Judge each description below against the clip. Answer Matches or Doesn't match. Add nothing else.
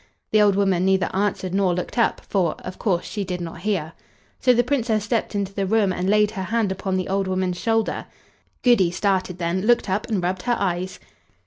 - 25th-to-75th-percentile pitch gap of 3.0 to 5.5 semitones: Doesn't match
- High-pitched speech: Matches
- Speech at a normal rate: Doesn't match